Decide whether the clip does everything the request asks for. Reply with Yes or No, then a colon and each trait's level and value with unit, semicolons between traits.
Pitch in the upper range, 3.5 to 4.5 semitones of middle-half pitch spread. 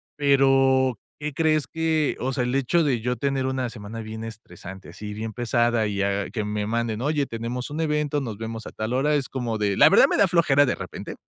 No: low, 125 Hz; average, 4.0 semitones